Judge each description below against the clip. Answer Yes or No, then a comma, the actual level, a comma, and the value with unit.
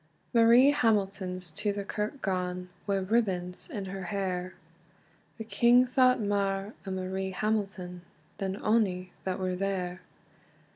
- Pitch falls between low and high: No, high, 195 Hz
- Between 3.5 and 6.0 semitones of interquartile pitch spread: No, average, 2.8 semitones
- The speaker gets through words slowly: Yes, slow, 130 wpm